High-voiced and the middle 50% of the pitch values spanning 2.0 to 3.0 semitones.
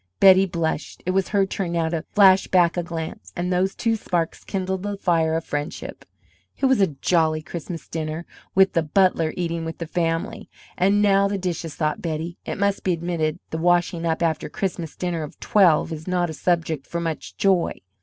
No: medium, 170 Hz; average, 2.7 semitones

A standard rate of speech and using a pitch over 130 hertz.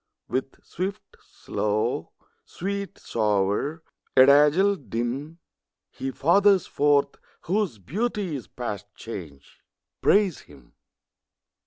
No: slow, 85 wpm; medium, 140 Hz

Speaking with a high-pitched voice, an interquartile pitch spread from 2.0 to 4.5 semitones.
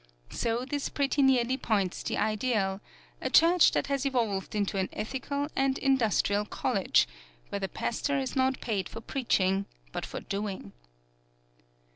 No: high, 235 Hz; average, 5.0 semitones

